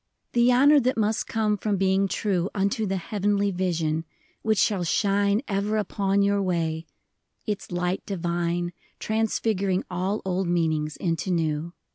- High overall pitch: Yes, high, 195 Hz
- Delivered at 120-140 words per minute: No, average, 150 wpm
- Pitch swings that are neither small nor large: Yes, average, 3.1 semitones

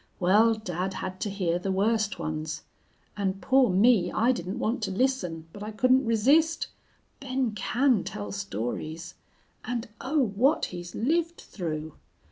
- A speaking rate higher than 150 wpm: No, average, 145 wpm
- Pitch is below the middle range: No, high, 205 Hz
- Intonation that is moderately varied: No, wide, 6.1 semitones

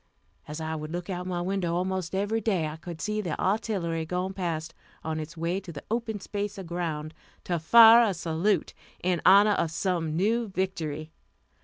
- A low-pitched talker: No, medium, 180 Hz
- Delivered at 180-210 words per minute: Yes, average, 185 wpm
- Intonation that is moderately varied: Yes, average, 3.6 semitones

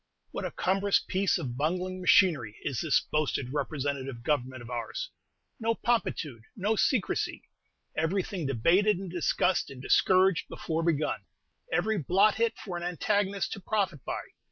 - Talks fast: No, average, 145 wpm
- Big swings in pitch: Yes, wide, 5.9 semitones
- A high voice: No, medium, 175 Hz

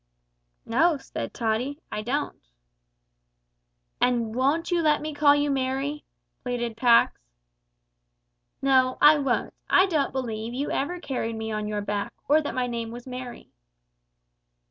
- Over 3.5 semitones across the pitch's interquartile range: Yes, average, 4.0 semitones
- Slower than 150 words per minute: Yes, average, 140 wpm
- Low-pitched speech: No, very high, 255 Hz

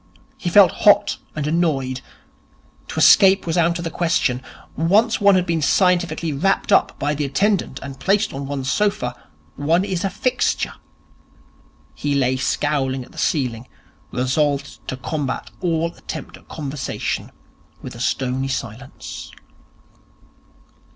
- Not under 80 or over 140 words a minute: Yes, slow, 135 wpm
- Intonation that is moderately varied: Yes, average, 4.9 semitones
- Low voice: No, medium, 150 Hz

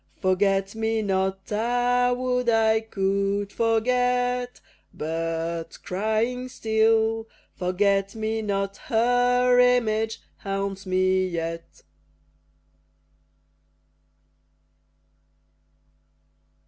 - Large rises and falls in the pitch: No, average, 3.9 semitones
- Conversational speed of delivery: No, slow, 70 wpm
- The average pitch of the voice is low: No, high, 220 Hz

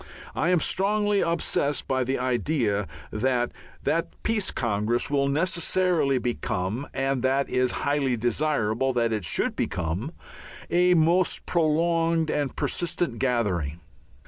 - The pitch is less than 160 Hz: Yes, low, 135 Hz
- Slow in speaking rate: Yes, slow, 125 wpm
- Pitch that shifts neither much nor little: No, wide, 5.9 semitones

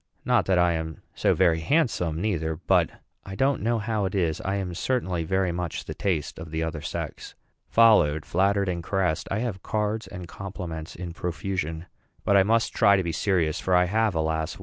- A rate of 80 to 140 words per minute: No, average, 195 wpm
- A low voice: Yes, very low, 90 Hz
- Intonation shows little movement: No, average, 3.6 semitones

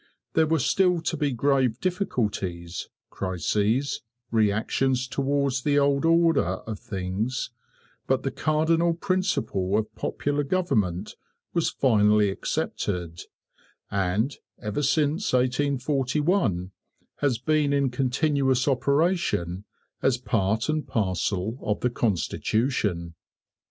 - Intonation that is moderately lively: No, wide, 6.0 semitones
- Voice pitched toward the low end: Yes, low, 130 Hz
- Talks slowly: Yes, slow, 105 wpm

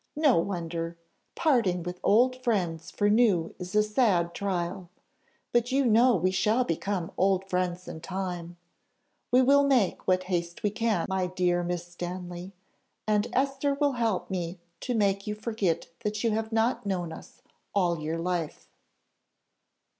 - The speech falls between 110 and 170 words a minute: Yes, average, 155 wpm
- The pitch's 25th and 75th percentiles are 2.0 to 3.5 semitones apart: No, average, 4.4 semitones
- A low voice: No, high, 190 Hz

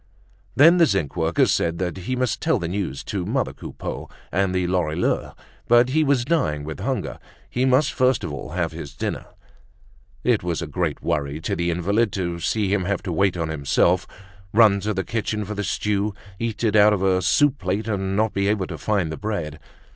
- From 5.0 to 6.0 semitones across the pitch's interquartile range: No, average, 4.3 semitones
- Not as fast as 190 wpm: No, fast, 205 wpm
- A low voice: Yes, very low, 95 Hz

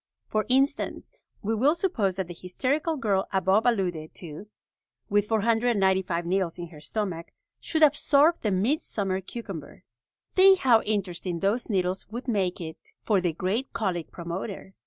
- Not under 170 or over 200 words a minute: No, average, 145 wpm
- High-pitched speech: Yes, high, 200 Hz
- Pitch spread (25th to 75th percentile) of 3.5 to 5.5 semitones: Yes, average, 4.7 semitones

